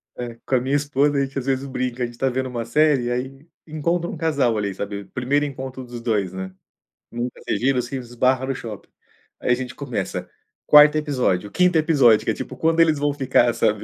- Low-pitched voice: Yes, low, 130 Hz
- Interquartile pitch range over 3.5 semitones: No, average, 3.2 semitones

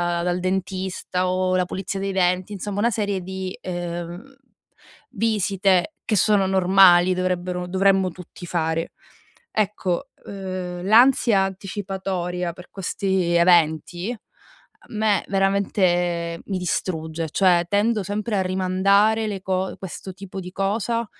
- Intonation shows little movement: Yes, narrow, 1.9 semitones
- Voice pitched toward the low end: No, high, 190 Hz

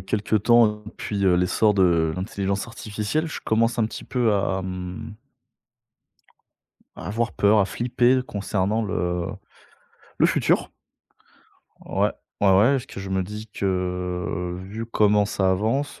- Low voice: Yes, low, 100 Hz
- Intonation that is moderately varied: Yes, average, 3.1 semitones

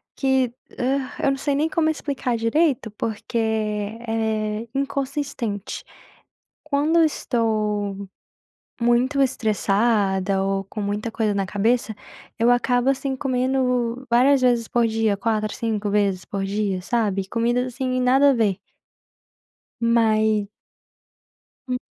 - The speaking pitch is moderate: No, high, 230 Hz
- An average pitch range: Yes, average, 3.5 semitones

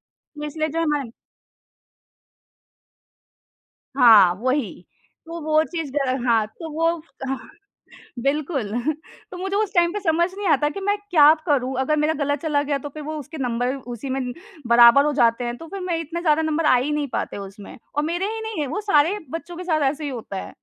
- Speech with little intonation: No, average, 4.2 semitones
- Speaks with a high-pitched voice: Yes, very high, 300 Hz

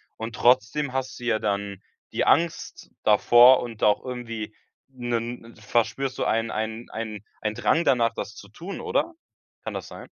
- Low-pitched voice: Yes, low, 115 Hz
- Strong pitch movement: No, average, 2.7 semitones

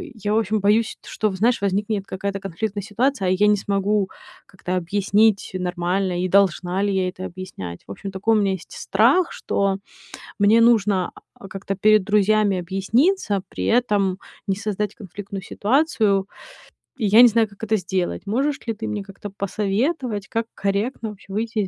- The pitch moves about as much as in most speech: No, narrow, 2.2 semitones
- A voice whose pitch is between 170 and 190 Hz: No, high, 200 Hz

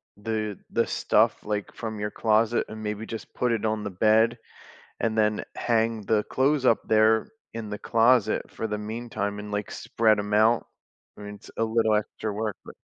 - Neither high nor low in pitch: No, low, 110 Hz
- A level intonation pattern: Yes, narrow, 1.3 semitones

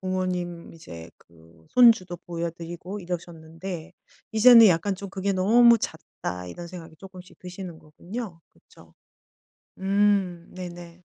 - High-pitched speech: No, medium, 180 Hz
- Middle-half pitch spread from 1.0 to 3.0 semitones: Yes, narrow, 2.6 semitones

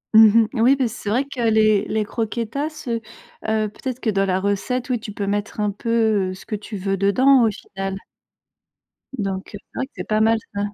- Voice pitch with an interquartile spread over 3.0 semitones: No, average, 2.7 semitones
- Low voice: No, high, 220 Hz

